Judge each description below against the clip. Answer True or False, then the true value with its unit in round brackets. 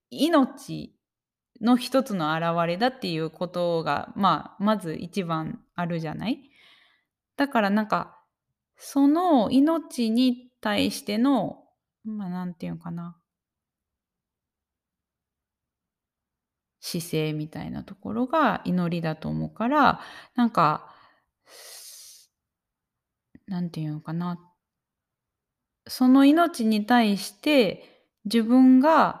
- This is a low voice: False (200 Hz)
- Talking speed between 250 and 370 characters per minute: False (185 characters per minute)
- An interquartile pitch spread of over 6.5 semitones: True (7.3 semitones)